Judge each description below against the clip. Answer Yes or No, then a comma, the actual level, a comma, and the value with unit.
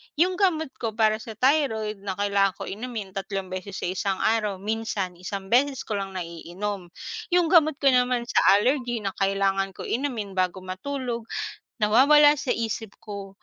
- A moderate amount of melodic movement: Yes, average, 4.5 semitones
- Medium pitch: No, high, 215 Hz